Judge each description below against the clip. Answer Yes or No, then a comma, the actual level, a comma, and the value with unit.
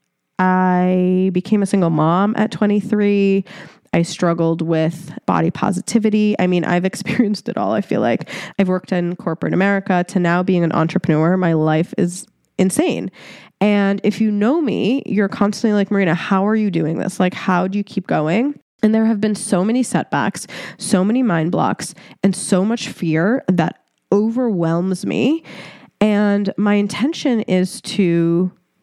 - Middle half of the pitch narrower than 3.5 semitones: Yes, average, 2.9 semitones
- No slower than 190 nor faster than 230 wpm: No, average, 160 wpm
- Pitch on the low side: No, high, 195 Hz